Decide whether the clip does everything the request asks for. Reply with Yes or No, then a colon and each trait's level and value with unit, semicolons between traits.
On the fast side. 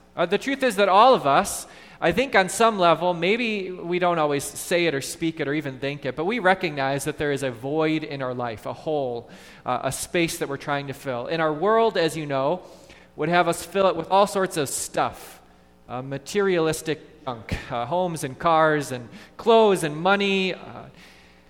Yes: fast, 210 wpm